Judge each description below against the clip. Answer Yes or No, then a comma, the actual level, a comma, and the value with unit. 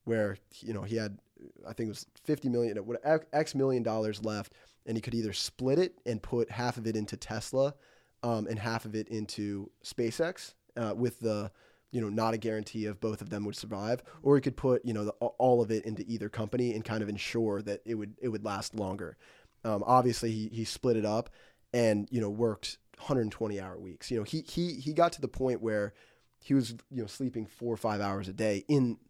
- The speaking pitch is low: Yes, low, 115 Hz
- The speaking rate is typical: No, fast, 225 wpm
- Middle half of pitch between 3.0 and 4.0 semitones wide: No, narrow, 2.5 semitones